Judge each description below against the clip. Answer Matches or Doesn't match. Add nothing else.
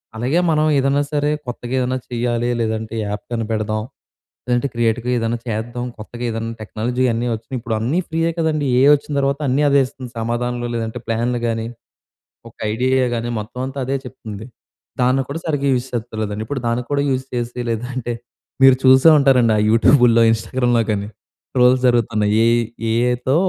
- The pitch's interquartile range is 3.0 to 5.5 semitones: Doesn't match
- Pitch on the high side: Doesn't match